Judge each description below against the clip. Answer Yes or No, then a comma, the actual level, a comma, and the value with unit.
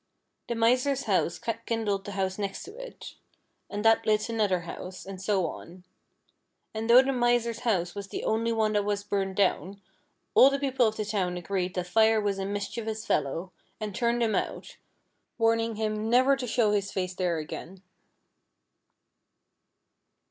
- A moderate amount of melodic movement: Yes, average, 3.1 semitones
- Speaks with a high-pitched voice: Yes, high, 210 Hz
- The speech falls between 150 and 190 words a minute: Yes, average, 165 wpm